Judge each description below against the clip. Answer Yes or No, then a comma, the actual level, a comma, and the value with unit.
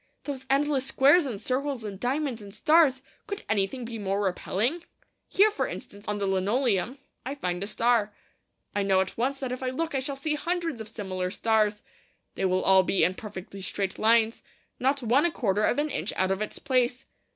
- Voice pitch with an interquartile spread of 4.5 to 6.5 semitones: Yes, wide, 5.5 semitones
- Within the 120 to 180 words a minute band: No, average, 200 wpm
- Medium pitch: No, high, 235 Hz